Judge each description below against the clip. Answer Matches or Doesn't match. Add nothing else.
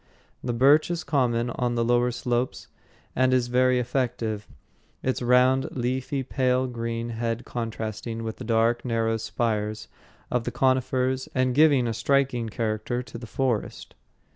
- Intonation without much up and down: Matches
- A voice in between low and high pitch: Doesn't match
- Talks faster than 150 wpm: Doesn't match